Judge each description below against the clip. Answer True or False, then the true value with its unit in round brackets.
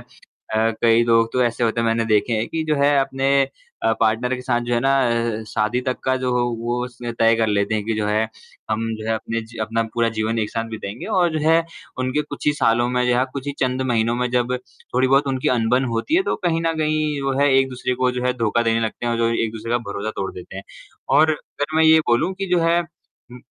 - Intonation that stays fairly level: False (3.1 semitones)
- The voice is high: False (120 Hz)